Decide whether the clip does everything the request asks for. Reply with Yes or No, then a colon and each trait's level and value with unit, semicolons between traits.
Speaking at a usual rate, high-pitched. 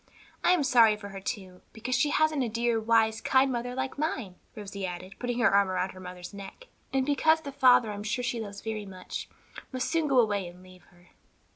No: fast, 225 wpm; high, 225 Hz